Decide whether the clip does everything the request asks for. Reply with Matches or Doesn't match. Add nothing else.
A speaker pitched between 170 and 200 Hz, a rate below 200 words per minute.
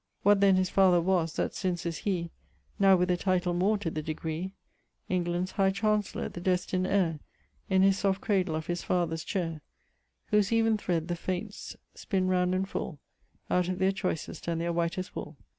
Matches